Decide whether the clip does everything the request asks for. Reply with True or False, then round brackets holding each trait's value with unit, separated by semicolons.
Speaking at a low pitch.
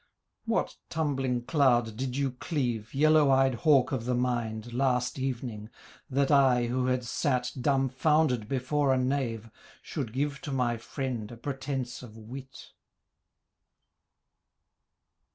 True (130 Hz)